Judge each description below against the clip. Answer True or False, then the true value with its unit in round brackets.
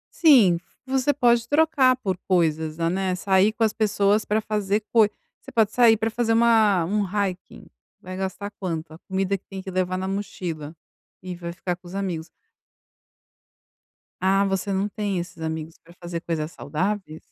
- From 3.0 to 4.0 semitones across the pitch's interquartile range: True (3.5 semitones)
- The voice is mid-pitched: False (195 Hz)